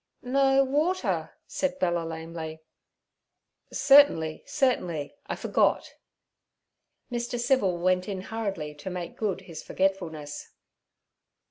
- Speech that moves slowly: Yes, slow, 100 wpm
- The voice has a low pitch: No, high, 190 Hz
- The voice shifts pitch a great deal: Yes, wide, 7.7 semitones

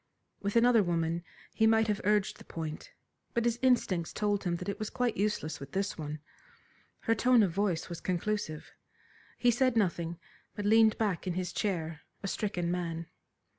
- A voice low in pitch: No, high, 200 Hz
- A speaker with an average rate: Yes, average, 175 wpm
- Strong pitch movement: No, average, 4.5 semitones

